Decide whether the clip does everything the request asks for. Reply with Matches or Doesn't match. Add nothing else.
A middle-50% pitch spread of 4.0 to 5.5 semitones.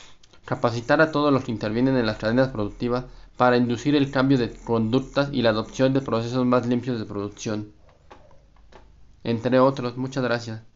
Doesn't match